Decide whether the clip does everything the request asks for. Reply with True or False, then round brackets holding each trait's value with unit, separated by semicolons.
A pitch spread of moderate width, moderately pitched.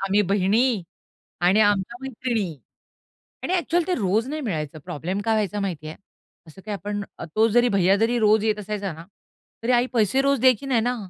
False (3.9 semitones; 210 Hz)